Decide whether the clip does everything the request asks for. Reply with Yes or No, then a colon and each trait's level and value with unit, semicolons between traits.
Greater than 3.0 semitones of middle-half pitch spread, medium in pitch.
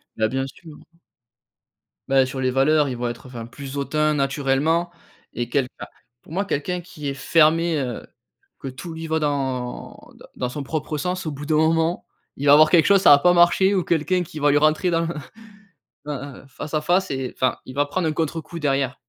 Yes: average, 3.4 semitones; medium, 150 Hz